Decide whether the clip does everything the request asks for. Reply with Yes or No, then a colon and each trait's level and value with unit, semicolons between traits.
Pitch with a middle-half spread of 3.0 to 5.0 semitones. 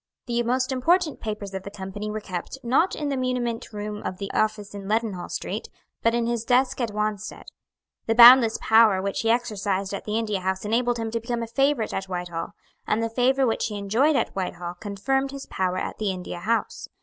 Yes: average, 3.5 semitones